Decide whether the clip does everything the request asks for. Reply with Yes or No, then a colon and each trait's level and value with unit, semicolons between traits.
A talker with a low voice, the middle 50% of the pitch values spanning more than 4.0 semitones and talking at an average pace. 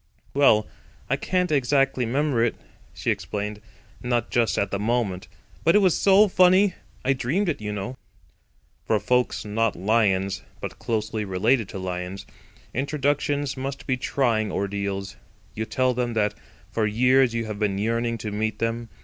Yes: low, 115 Hz; average, 4.4 semitones; average, 160 wpm